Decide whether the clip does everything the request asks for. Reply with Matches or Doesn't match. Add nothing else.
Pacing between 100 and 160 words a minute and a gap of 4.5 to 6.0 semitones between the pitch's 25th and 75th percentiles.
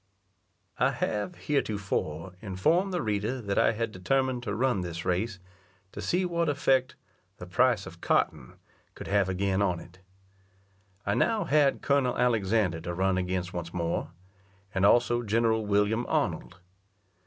Matches